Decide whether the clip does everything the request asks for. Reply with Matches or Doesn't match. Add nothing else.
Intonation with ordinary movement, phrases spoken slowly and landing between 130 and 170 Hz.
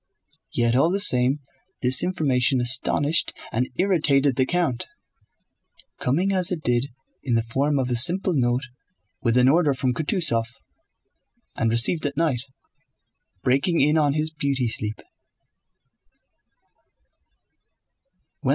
Matches